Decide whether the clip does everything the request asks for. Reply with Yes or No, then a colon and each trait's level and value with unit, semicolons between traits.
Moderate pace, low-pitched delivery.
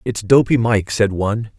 Yes: average, 190 wpm; low, 110 Hz